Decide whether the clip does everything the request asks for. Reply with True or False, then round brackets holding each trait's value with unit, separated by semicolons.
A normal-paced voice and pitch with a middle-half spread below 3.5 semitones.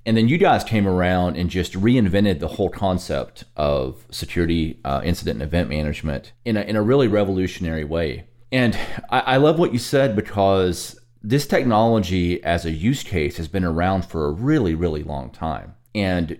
False (185 wpm; 5.3 semitones)